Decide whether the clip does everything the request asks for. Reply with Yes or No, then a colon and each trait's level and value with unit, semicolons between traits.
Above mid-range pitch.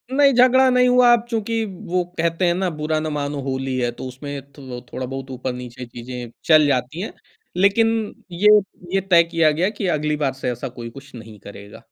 No: medium, 150 Hz